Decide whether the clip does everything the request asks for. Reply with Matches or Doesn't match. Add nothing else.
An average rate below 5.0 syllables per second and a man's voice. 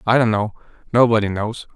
Doesn't match